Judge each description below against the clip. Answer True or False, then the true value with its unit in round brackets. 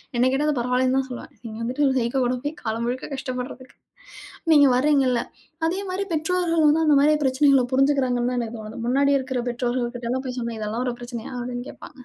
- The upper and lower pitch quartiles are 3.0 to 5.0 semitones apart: False (2.6 semitones)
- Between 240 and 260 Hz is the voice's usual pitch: True (255 Hz)